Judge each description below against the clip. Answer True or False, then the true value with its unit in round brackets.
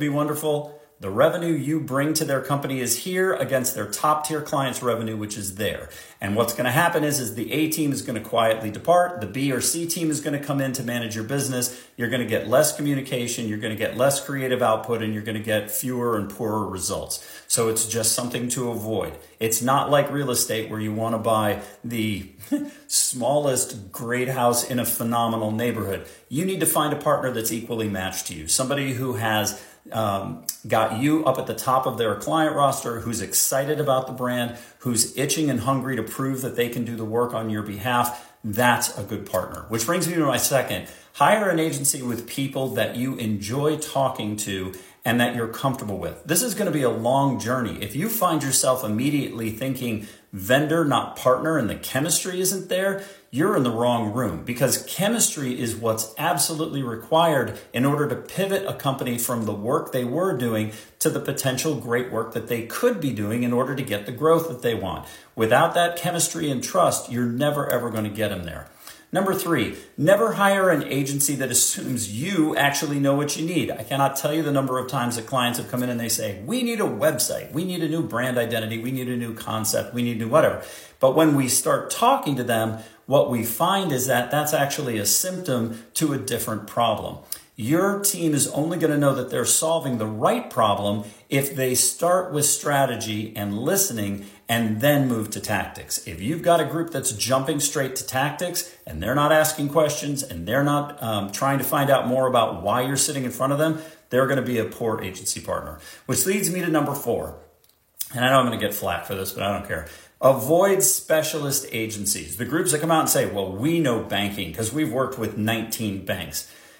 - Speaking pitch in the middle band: False (125 Hz)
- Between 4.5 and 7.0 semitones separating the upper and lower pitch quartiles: True (4.9 semitones)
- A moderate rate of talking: False (215 wpm)